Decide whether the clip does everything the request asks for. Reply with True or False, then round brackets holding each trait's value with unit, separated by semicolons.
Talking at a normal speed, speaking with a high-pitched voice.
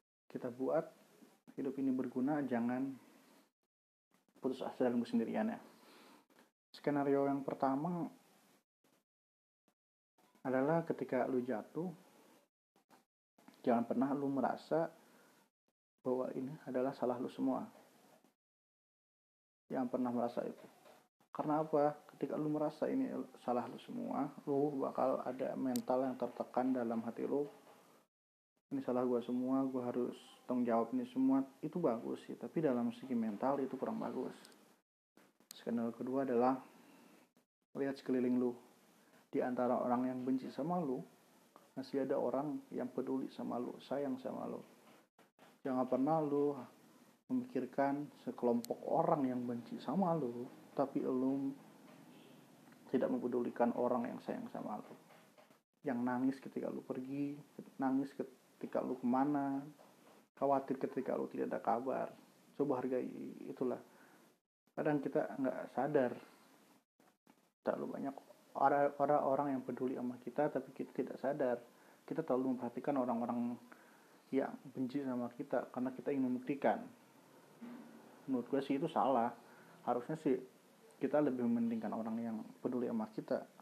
False (125 wpm; 135 Hz)